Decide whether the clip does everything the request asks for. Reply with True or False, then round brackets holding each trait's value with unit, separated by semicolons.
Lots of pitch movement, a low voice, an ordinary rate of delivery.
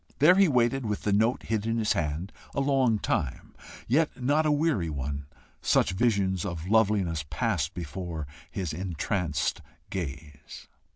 True (6.9 semitones; 100 Hz; 150 wpm)